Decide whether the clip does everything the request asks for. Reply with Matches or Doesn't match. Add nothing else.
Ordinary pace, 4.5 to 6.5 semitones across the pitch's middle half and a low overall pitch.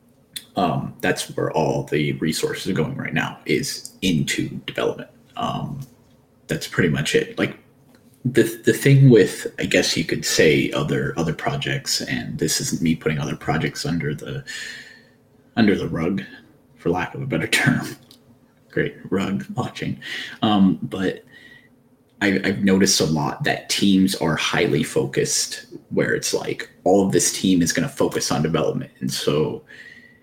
Matches